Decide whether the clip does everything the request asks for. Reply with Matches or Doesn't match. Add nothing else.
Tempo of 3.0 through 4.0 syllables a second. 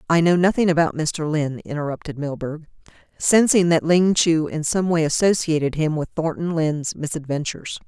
Doesn't match